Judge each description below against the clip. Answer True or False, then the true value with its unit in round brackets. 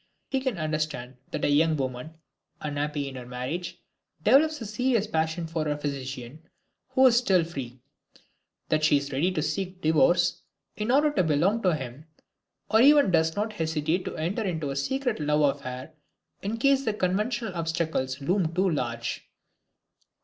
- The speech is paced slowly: False (165 wpm)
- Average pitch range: False (5.9 semitones)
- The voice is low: False (160 Hz)